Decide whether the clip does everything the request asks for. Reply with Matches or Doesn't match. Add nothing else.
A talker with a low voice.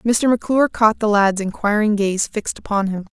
Doesn't match